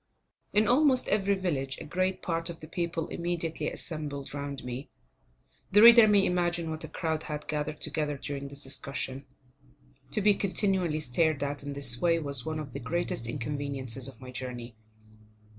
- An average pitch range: Yes, average, 4.0 semitones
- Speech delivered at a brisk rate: No, average, 170 wpm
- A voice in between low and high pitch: Yes, medium, 155 Hz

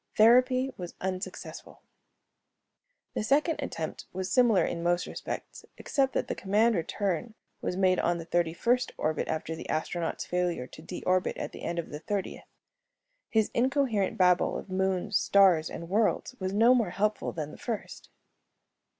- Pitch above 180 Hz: Yes, high, 190 Hz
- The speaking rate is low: No, average, 160 wpm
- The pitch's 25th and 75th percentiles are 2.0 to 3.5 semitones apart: No, average, 4.7 semitones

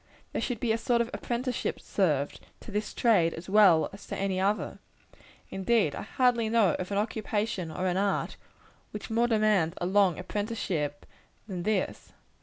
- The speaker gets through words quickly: No, average, 170 wpm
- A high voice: Yes, high, 205 Hz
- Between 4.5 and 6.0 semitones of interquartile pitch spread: No, average, 3.6 semitones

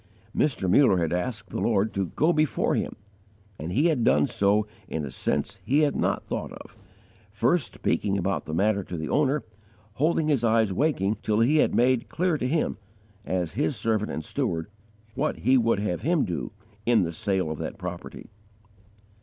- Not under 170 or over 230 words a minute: Yes, average, 185 wpm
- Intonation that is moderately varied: No, wide, 7.0 semitones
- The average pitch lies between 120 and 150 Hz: No, low, 110 Hz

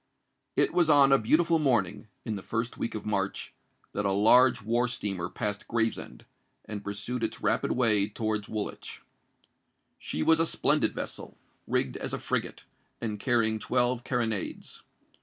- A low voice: Yes, low, 115 Hz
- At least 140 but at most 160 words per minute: Yes, average, 155 wpm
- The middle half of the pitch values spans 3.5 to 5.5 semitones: No, average, 3.1 semitones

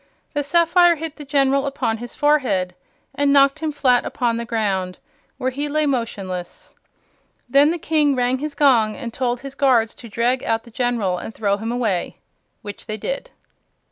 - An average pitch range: Yes, average, 4.3 semitones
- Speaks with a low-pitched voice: No, very high, 255 Hz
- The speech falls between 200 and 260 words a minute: No, average, 175 wpm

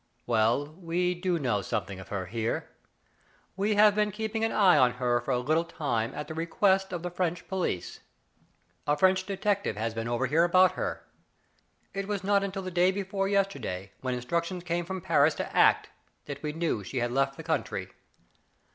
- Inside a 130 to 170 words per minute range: No, average, 190 wpm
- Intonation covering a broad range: Yes, wide, 7.3 semitones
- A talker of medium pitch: Yes, medium, 170 Hz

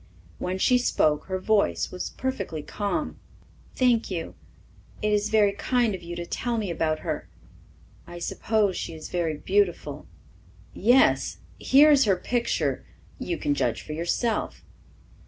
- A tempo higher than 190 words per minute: No, average, 145 wpm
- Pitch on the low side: No, high, 205 Hz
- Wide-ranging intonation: Yes, wide, 5.8 semitones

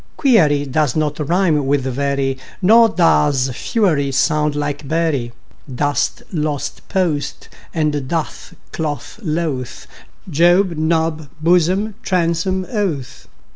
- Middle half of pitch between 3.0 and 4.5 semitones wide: Yes, average, 3.5 semitones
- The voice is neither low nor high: Yes, medium, 155 Hz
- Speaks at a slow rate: Yes, slow, 105 wpm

